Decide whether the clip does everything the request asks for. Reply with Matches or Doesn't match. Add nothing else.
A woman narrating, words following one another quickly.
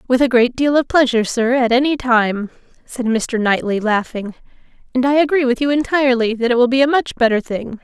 Matches